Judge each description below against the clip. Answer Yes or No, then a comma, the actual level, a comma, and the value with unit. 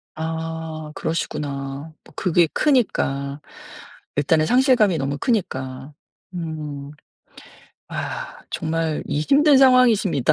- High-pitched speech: No, medium, 160 Hz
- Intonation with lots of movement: Yes, wide, 6.4 semitones